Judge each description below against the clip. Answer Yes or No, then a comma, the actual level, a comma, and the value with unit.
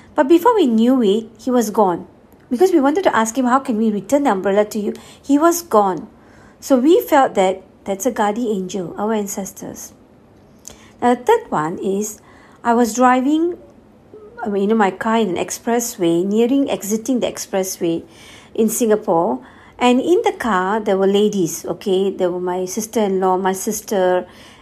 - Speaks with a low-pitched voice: No, high, 220 Hz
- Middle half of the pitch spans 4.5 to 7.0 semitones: Yes, average, 4.8 semitones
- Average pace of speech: Yes, average, 170 wpm